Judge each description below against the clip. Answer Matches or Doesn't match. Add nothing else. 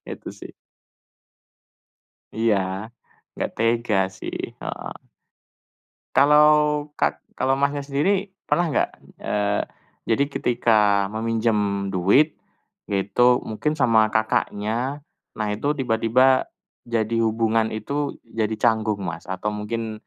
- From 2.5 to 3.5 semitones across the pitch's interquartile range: Doesn't match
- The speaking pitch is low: Matches